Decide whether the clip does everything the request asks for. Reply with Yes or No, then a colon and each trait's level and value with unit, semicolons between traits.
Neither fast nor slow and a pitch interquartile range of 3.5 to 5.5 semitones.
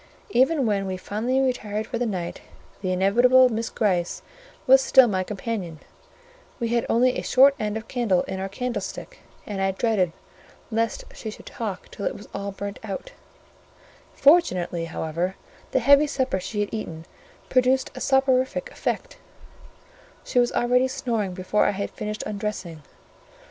Yes: average, 155 wpm; average, 4.8 semitones